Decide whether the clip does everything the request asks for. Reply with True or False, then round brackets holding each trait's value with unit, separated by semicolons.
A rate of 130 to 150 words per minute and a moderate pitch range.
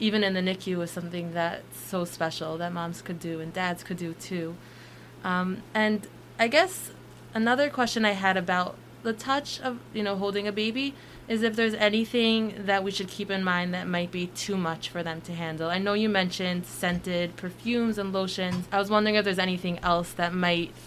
False (205 wpm; 3.4 semitones)